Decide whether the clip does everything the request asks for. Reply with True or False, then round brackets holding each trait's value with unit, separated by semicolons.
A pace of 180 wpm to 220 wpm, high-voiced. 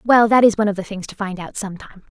False (305 wpm; 205 Hz)